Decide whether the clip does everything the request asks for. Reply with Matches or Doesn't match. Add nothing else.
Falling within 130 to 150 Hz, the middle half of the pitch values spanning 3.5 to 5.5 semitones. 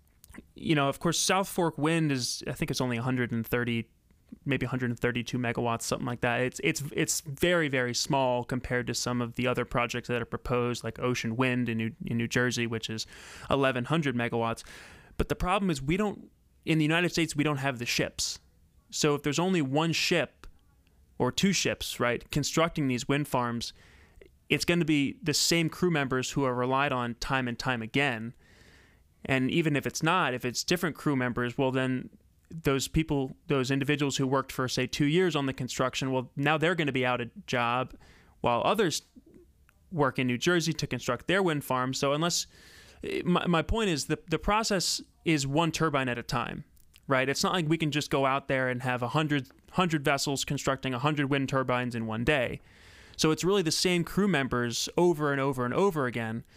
Matches